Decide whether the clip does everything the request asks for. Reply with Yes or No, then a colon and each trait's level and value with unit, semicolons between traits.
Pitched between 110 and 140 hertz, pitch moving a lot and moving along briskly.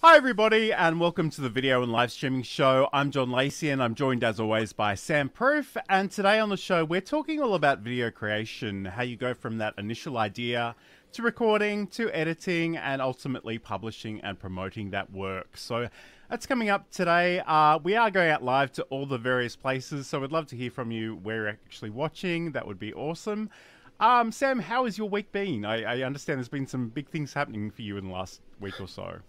Yes: low, 135 Hz; wide, 8.1 semitones; fast, 215 wpm